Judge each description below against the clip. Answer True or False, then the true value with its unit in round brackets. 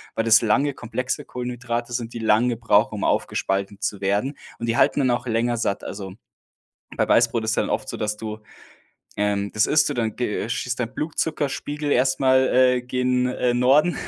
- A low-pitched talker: True (120 Hz)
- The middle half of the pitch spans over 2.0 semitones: True (2.6 semitones)